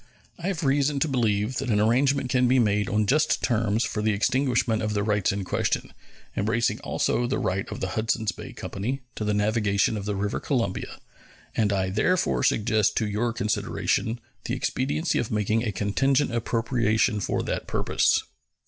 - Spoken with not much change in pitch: No, average, 3.6 semitones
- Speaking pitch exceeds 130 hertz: No, low, 110 Hz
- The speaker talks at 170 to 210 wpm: Yes, average, 175 wpm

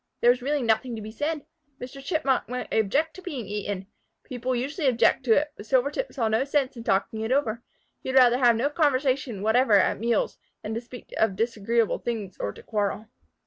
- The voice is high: Yes, high, 245 Hz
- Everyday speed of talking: No, fast, 210 wpm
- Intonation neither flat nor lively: Yes, average, 3.6 semitones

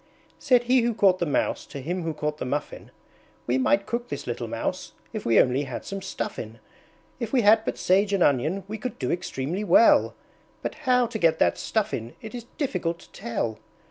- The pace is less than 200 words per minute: No, fast, 205 wpm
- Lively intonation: Yes, wide, 8.0 semitones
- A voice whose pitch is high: Yes, high, 195 Hz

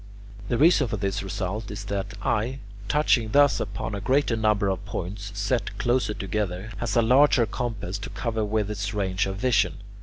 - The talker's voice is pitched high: No, low, 105 Hz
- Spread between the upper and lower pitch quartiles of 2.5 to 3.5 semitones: Yes, average, 3.2 semitones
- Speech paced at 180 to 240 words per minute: Yes, average, 185 wpm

